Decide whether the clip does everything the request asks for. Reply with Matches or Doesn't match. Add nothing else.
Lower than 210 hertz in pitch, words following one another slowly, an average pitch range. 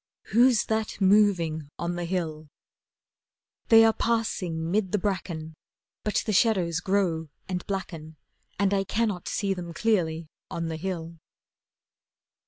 Matches